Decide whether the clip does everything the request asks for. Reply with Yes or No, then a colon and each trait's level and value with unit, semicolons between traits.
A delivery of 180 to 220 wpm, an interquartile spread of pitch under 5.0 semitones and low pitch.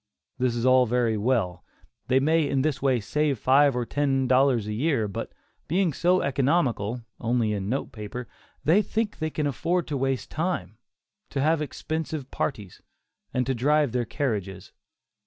No: average, 165 wpm; average, 4.3 semitones; low, 130 Hz